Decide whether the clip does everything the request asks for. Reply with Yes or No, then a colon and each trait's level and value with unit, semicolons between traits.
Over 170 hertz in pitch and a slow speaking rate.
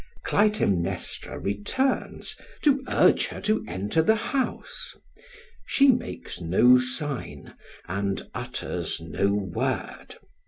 No: low, 125 Hz; slow, 95 wpm